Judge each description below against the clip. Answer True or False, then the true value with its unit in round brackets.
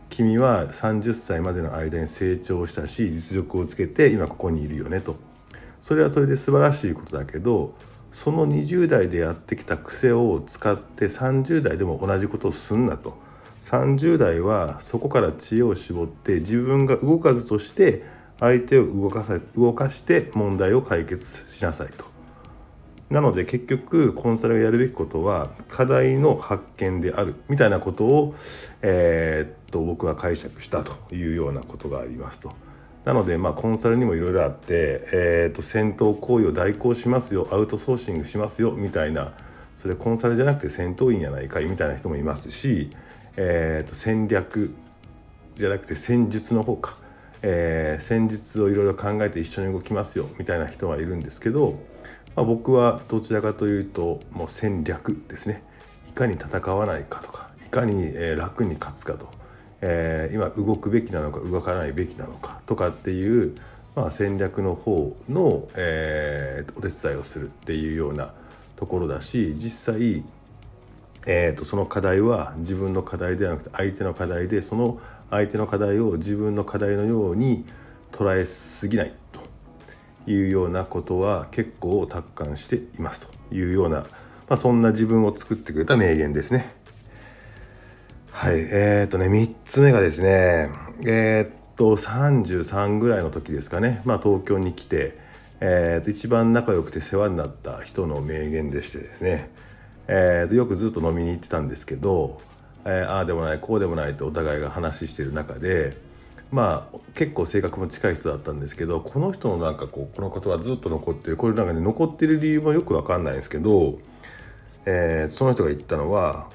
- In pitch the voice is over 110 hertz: False (100 Hz)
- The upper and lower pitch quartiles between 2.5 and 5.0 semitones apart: False (5.6 semitones)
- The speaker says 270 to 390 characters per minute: True (335 characters per minute)